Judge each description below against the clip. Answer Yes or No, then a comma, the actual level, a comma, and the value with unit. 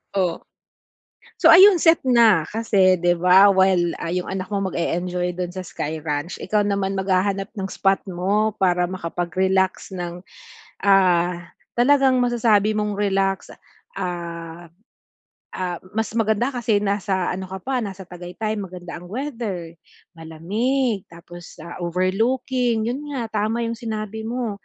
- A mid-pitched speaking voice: No, high, 195 Hz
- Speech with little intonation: No, average, 3.6 semitones